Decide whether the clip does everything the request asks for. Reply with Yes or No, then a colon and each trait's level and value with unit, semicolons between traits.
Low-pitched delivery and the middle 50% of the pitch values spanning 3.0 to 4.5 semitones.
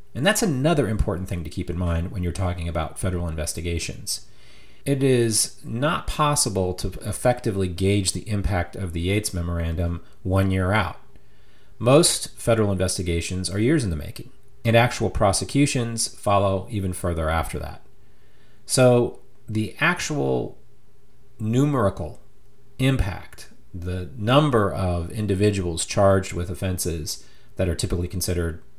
No: low, 100 Hz; average, 5.1 semitones